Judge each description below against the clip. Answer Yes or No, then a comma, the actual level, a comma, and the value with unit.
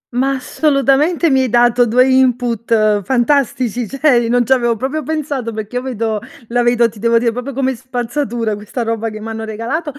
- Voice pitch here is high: Yes, high, 245 Hz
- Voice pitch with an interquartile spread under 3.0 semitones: Yes, narrow, 2.6 semitones